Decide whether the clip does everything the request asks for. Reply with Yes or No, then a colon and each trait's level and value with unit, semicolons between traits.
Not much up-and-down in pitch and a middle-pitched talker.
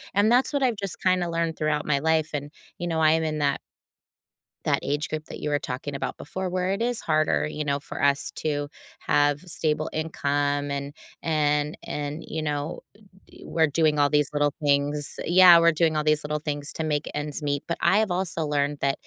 Yes: narrow, 2.2 semitones; medium, 150 Hz